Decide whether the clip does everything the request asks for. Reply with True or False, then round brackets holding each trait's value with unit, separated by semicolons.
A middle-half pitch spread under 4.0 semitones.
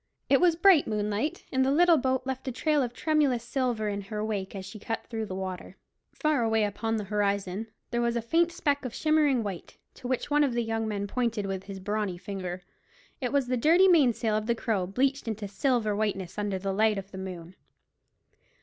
False (4.6 semitones)